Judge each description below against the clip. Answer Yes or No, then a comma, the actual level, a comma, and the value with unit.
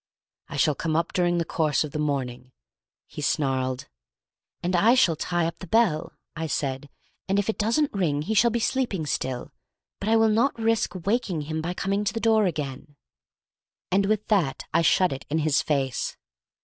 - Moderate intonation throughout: No, wide, 6.5 semitones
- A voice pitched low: No, medium, 170 Hz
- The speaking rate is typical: Yes, average, 190 wpm